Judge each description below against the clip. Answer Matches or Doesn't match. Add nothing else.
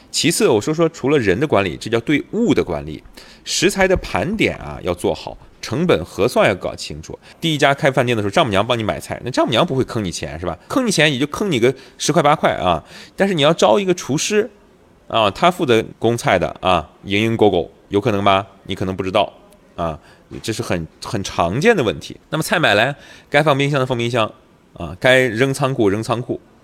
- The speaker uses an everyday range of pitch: Doesn't match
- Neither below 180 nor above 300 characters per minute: Doesn't match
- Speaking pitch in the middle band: Doesn't match